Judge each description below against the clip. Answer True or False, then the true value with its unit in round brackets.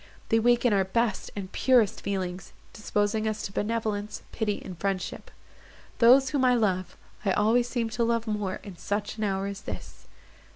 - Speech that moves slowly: False (165 wpm)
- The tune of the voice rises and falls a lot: False (2.8 semitones)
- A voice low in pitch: False (210 Hz)